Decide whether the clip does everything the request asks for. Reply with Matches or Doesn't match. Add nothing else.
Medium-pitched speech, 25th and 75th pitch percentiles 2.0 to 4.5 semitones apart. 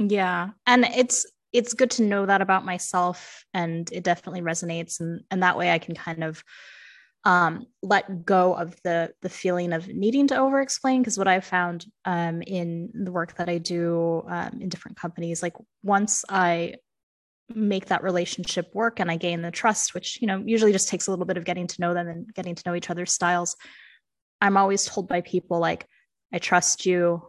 Matches